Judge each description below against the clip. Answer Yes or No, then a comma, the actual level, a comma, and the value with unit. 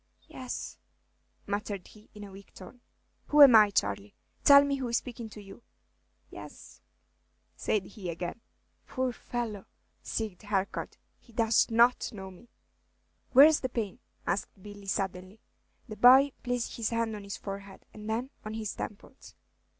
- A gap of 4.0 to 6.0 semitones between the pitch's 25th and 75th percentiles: No, average, 3.4 semitones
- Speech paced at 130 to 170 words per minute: Yes, average, 150 wpm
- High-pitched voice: Yes, high, 215 Hz